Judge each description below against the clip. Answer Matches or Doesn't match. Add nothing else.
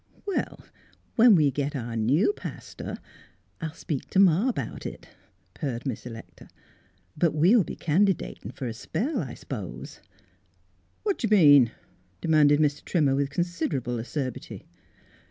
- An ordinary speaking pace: Matches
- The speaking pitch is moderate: Matches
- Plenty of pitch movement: Matches